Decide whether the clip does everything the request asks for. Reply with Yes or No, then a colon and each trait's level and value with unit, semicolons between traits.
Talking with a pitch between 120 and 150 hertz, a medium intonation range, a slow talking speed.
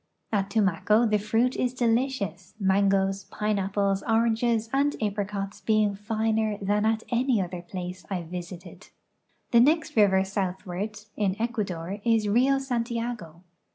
No: high, 210 Hz; average, 3.1 semitones; slow, 125 wpm